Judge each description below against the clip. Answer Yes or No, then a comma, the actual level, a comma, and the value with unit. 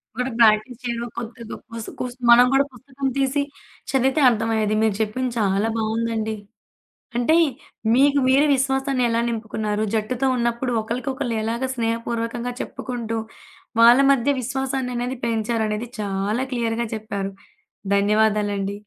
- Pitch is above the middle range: Yes, high, 235 Hz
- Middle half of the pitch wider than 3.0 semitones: No, average, 2.7 semitones